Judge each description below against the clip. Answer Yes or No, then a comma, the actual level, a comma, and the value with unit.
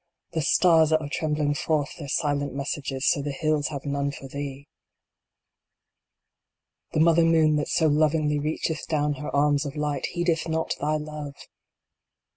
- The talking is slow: No, average, 155 wpm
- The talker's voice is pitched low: No, medium, 150 Hz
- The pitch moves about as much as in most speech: No, narrow, 1.7 semitones